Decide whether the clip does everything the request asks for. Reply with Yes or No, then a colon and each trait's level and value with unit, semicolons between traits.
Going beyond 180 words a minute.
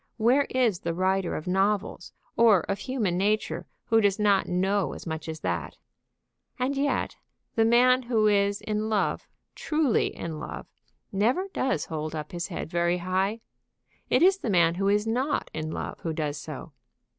No: average, 170 wpm